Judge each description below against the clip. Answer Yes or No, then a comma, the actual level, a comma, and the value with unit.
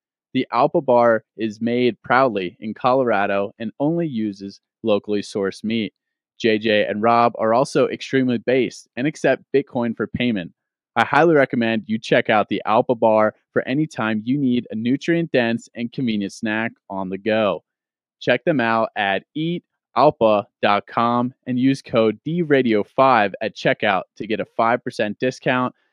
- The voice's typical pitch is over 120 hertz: No, low, 115 Hz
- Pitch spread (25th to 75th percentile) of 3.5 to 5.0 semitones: No, average, 3.1 semitones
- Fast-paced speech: No, average, 150 wpm